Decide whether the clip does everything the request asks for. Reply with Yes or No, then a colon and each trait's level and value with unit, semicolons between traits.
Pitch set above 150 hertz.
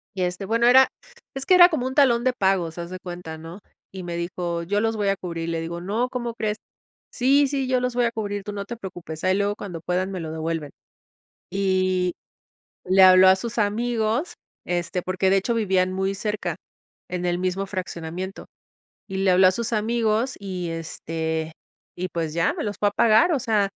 Yes: high, 190 Hz